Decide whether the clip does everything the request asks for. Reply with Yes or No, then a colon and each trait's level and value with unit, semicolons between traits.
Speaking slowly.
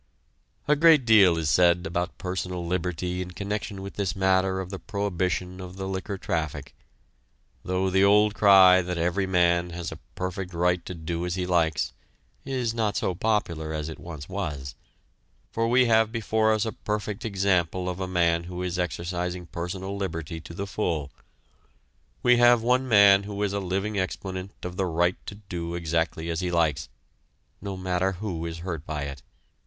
No: average, 180 wpm